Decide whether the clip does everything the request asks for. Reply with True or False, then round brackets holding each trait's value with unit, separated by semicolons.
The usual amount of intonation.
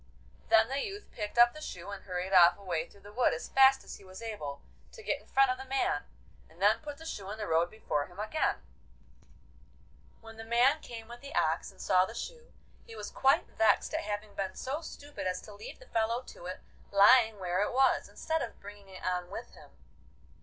False (5.8 semitones)